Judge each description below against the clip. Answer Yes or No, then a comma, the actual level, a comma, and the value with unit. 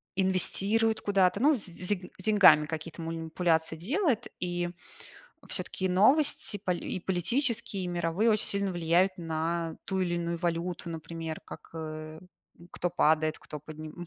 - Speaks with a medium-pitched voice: Yes, medium, 175 Hz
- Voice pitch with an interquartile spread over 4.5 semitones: No, average, 3.5 semitones